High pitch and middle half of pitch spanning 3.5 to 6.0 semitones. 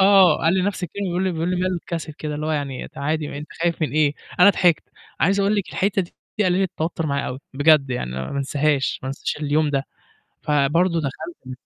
No: medium, 155 Hz; average, 4.0 semitones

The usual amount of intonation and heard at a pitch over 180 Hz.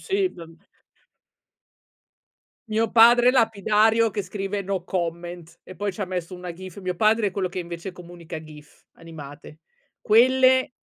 Yes: average, 4.5 semitones; high, 190 Hz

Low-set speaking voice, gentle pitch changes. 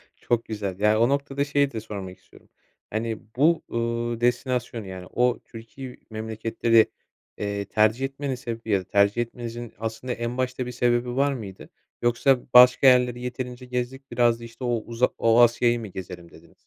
Yes: low, 120 Hz; narrow, 2.0 semitones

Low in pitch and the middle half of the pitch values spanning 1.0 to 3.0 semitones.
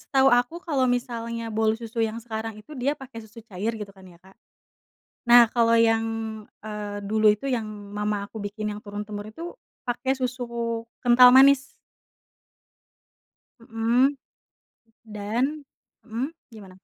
No: high, 230 Hz; narrow, 2.6 semitones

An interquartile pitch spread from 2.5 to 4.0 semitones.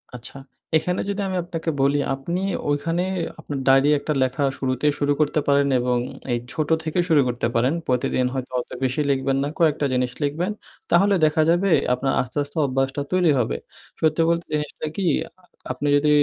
Yes: average, 3.7 semitones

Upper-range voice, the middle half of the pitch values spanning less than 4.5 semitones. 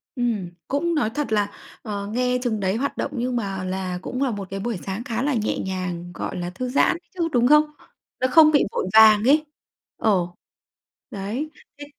No: high, 220 Hz; average, 5.3 semitones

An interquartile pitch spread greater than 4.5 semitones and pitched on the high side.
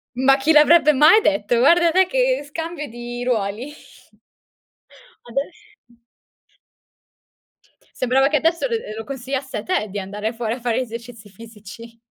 Yes: average, 5.1 semitones; very high, 255 Hz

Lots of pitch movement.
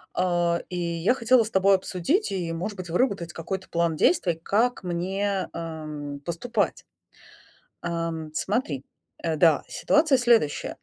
No: average, 3.5 semitones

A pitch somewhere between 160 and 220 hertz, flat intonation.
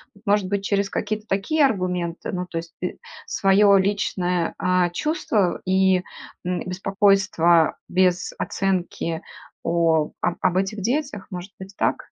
Yes: high, 190 Hz; narrow, 2.1 semitones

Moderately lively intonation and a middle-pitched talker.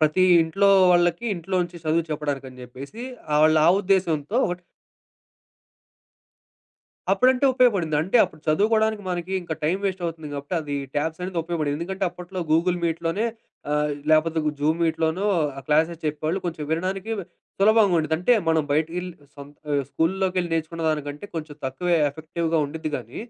Yes: average, 3.1 semitones; medium, 165 Hz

